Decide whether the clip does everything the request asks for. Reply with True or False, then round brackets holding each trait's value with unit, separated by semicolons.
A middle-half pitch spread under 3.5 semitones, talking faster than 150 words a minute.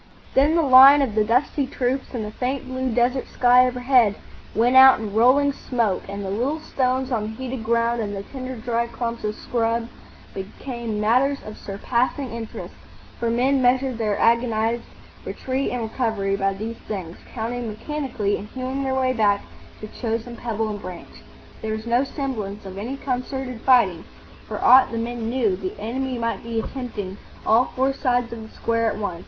True (3.0 semitones; 180 wpm)